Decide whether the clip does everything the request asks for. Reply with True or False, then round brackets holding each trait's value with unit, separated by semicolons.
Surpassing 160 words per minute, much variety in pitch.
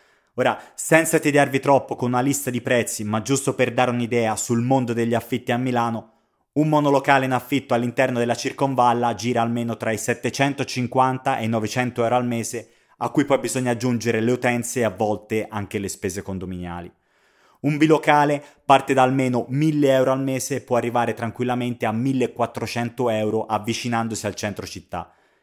False (170 wpm; 2.6 semitones)